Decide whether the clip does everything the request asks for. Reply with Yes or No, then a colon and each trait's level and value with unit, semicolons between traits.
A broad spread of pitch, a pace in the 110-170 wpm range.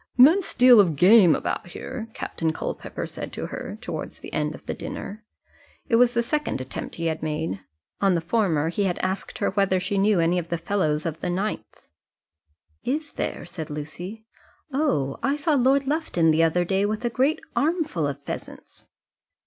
No: wide, 6.9 semitones; average, 185 wpm